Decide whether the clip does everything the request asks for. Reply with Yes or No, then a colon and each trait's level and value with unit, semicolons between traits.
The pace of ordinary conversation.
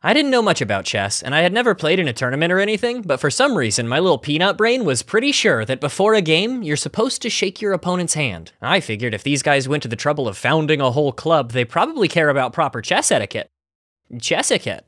No: fast, 245 wpm